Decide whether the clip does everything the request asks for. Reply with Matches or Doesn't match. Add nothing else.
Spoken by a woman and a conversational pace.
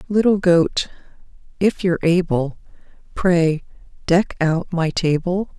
Doesn't match